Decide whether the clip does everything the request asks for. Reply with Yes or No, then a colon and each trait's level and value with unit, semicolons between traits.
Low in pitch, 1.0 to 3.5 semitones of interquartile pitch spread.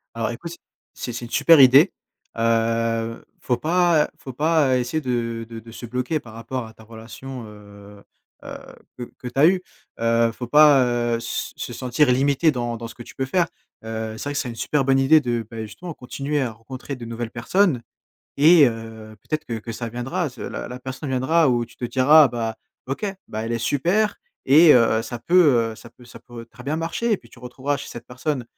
No: low, 125 Hz; average, 3.9 semitones